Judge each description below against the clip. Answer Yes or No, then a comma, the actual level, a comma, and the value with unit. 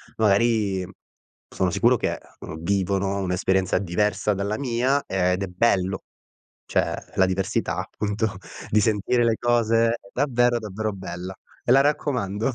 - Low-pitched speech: Yes, low, 105 Hz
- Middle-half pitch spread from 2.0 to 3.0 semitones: No, average, 3.6 semitones